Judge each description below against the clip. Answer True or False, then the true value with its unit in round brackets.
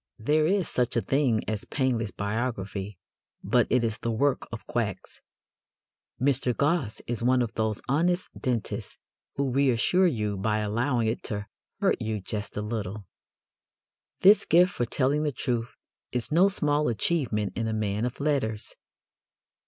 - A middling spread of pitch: True (4.7 semitones)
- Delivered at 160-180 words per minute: False (150 wpm)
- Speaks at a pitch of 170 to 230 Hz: False (120 Hz)